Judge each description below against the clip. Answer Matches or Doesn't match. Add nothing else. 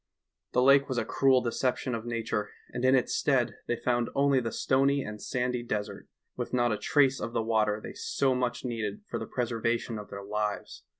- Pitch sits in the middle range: Doesn't match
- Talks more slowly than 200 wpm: Doesn't match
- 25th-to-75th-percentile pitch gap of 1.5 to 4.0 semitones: Matches